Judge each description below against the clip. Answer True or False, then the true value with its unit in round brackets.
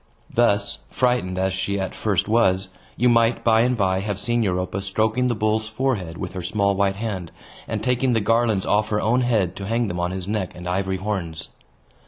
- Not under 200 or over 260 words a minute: True (205 wpm)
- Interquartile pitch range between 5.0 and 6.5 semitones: False (3.4 semitones)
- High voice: False (100 Hz)